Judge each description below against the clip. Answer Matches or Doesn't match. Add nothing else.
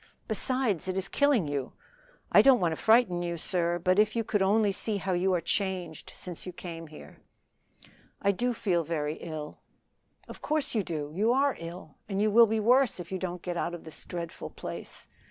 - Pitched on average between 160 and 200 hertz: Matches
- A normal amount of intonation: Matches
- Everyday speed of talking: Doesn't match